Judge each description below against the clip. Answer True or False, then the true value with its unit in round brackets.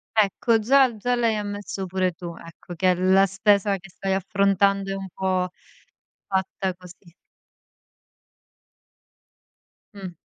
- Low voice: False (195 Hz)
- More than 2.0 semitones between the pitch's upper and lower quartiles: False (1.7 semitones)